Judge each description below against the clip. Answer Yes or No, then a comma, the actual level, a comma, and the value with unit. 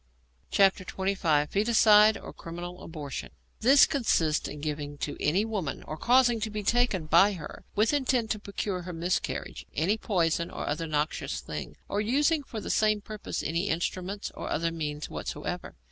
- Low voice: No, high, 190 Hz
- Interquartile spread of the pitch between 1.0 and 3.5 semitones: No, average, 5.1 semitones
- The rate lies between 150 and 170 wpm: Yes, average, 160 wpm